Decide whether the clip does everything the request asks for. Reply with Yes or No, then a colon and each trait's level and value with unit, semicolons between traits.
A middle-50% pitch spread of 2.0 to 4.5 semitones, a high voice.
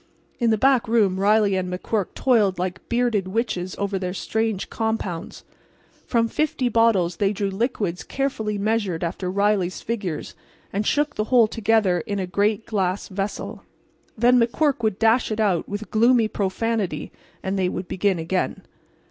Yes: average, 3.3 semitones; high, 210 Hz